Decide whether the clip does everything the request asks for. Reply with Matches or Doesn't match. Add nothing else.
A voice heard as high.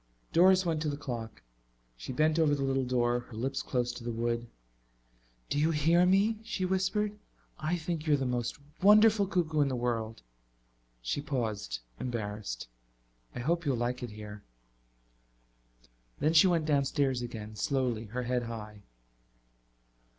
Doesn't match